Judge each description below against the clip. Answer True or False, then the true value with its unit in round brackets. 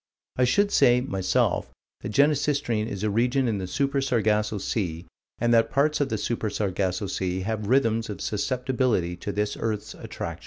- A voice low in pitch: True (110 Hz)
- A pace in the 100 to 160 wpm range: False (170 wpm)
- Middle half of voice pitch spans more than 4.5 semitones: False (4.1 semitones)